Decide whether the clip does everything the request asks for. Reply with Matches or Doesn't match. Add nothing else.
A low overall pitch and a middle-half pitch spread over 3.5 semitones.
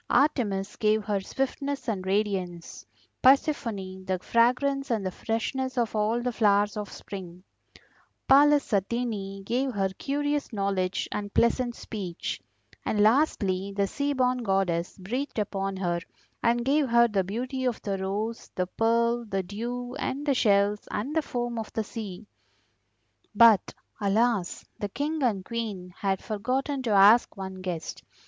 Doesn't match